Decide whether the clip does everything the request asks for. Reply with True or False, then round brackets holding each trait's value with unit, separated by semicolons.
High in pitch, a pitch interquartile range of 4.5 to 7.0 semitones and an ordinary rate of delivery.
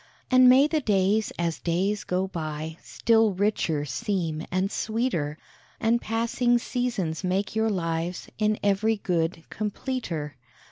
False (195 Hz; 5.1 semitones; 130 wpm)